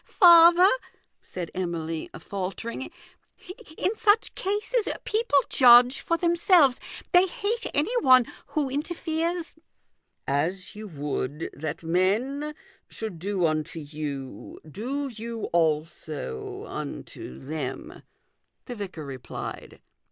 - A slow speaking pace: Yes, slow, 115 wpm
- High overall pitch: Yes, high, 220 Hz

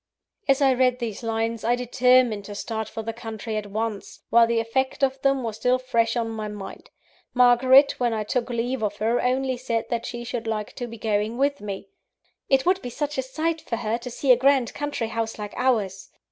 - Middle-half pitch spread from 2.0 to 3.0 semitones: Yes, narrow, 2.6 semitones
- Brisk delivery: Yes, fast, 215 wpm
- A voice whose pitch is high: Yes, high, 235 Hz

